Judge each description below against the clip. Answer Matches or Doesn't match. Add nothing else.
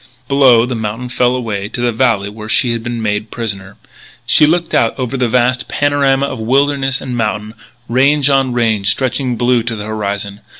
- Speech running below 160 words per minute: Doesn't match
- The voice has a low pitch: Matches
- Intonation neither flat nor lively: Matches